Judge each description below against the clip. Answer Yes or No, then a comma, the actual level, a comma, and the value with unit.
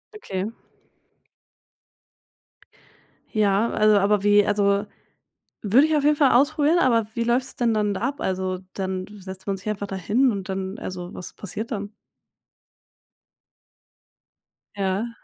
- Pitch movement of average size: Yes, average, 3.6 semitones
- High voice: Yes, high, 205 Hz